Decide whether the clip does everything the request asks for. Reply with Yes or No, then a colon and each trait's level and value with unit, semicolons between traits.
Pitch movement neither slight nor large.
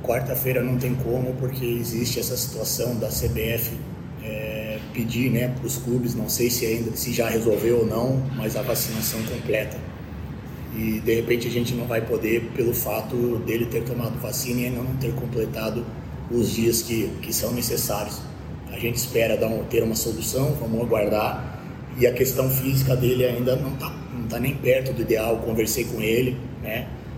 No: narrow, 1.8 semitones